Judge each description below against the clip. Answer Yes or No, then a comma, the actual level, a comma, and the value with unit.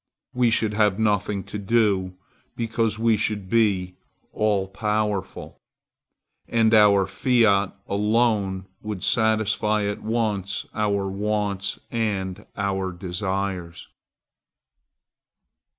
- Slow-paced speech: Yes, slow, 95 wpm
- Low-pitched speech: Yes, low, 105 Hz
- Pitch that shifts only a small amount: Yes, narrow, 2.2 semitones